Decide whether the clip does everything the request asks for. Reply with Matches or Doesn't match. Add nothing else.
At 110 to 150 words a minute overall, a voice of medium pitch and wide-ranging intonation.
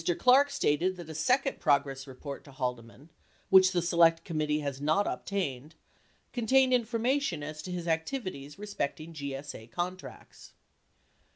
Matches